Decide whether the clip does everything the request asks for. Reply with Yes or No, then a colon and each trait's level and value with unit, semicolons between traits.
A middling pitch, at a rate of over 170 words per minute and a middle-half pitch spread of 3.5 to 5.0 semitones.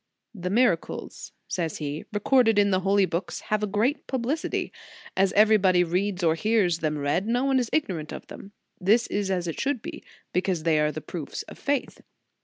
No: high, 195 Hz; average, 190 wpm; average, 4.5 semitones